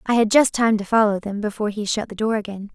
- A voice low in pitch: No, high, 215 Hz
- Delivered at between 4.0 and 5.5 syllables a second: No, 6.5 syllables/s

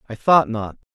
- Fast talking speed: No, average, 190 wpm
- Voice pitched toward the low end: Yes, low, 120 Hz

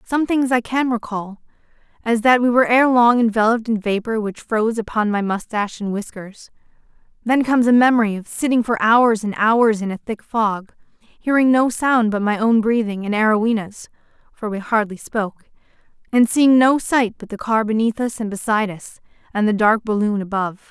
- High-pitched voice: Yes, high, 225 Hz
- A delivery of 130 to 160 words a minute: No, average, 185 wpm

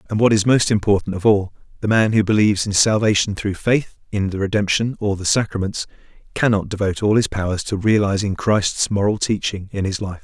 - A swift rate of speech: No, average, 195 wpm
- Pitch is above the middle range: No, low, 105 Hz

